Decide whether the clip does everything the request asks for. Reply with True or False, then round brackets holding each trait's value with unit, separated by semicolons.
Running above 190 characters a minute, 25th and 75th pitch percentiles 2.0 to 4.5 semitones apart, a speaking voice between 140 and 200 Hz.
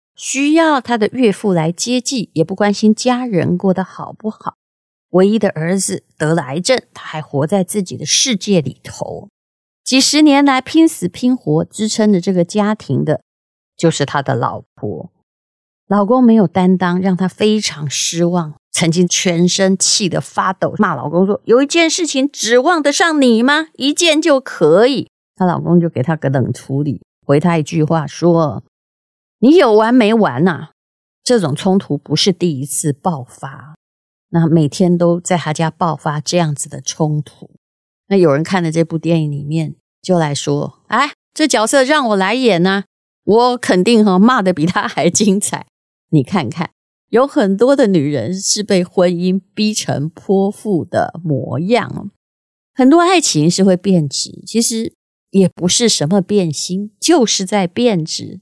False (235 characters per minute; 5.4 semitones; 185 Hz)